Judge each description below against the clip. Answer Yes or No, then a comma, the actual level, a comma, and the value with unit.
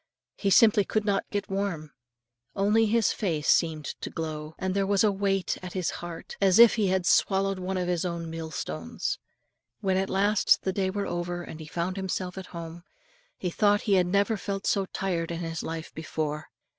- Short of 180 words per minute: No, average, 195 wpm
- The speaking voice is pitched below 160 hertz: No, medium, 185 Hz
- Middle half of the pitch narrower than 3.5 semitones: Yes, average, 3.0 semitones